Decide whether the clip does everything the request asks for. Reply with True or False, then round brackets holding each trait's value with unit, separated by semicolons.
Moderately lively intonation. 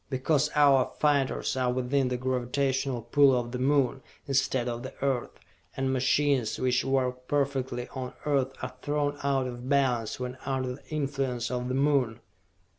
False (1.8 semitones)